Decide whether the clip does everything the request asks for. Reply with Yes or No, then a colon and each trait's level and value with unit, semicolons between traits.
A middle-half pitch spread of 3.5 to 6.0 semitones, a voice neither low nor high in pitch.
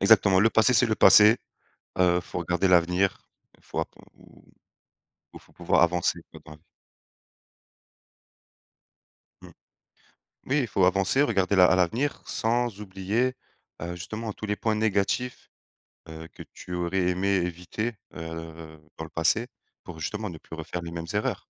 No: average, 4.0 semitones; very low, 95 Hz